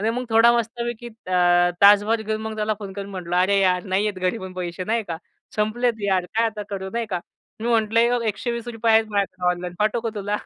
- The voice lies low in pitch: No, high, 210 Hz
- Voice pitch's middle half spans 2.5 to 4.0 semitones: Yes, average, 3.3 semitones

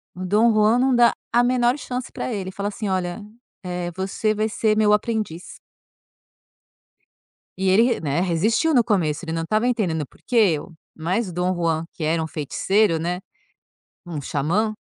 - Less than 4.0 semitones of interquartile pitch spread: No, average, 4.7 semitones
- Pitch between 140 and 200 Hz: Yes, high, 190 Hz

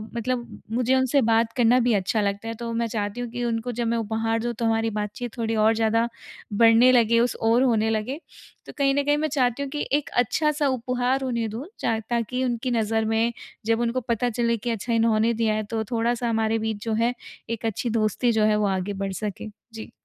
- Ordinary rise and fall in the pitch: No, narrow, 1.7 semitones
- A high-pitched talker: Yes, high, 230 Hz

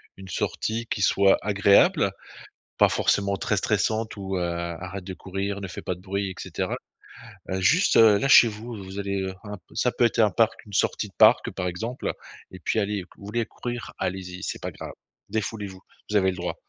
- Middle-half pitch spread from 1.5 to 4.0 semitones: Yes, narrow, 2.6 semitones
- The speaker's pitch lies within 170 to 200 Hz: No, low, 100 Hz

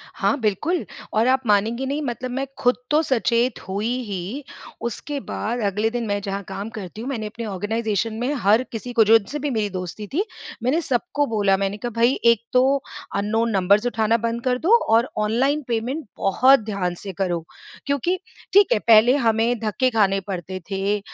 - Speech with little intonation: No, average, 3.8 semitones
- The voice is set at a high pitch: Yes, high, 225 Hz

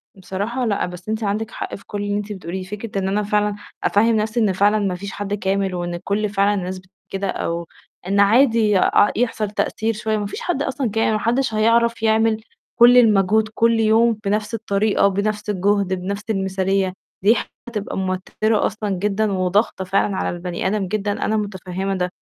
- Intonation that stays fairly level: Yes, narrow, 2.2 semitones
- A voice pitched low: No, high, 205 Hz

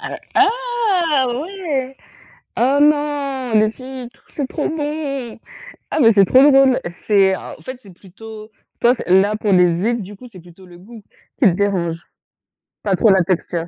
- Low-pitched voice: No, high, 235 Hz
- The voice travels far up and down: Yes, wide, 6.2 semitones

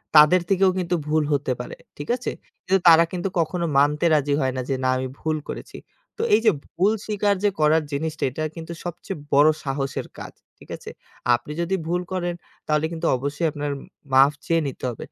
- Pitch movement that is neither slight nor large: Yes, average, 3.6 semitones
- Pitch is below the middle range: No, medium, 155 Hz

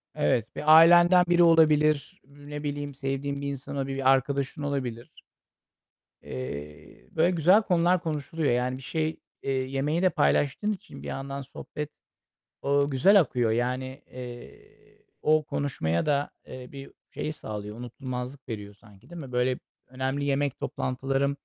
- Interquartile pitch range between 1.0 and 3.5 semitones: Yes, average, 3.1 semitones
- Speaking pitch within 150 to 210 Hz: No, medium, 140 Hz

